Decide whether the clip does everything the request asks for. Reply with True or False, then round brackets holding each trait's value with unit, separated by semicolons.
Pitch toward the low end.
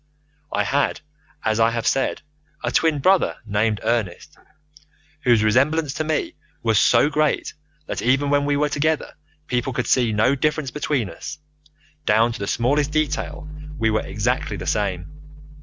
True (130 Hz)